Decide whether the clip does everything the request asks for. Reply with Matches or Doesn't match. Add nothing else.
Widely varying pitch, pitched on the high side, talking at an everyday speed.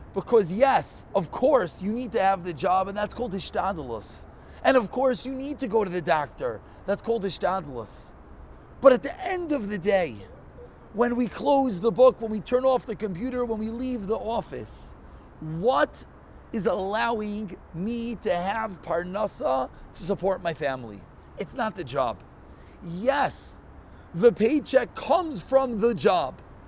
Matches